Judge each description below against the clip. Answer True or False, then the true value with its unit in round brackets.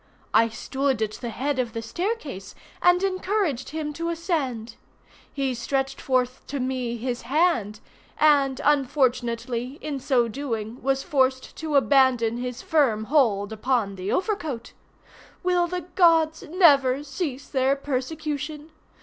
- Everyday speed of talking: False (130 wpm)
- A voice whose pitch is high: True (270 Hz)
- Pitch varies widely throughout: False (4.2 semitones)